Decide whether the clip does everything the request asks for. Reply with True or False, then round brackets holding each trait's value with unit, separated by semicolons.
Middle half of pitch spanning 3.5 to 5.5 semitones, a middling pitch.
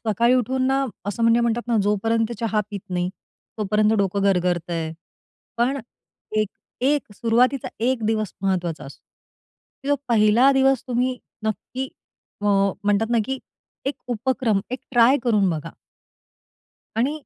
False (4.0 semitones; 225 Hz)